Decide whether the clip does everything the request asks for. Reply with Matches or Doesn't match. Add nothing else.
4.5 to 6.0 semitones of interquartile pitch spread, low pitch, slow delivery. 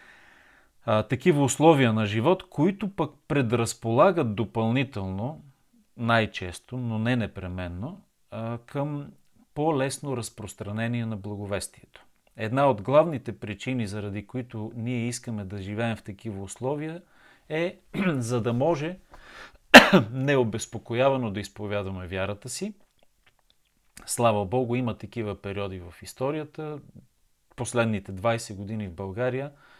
Matches